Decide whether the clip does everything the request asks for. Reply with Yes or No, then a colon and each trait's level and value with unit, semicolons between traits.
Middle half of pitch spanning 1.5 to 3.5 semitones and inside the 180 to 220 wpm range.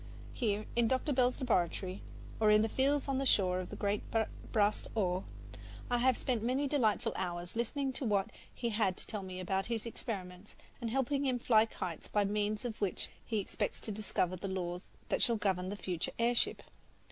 No: average, 4.2 semitones; average, 195 wpm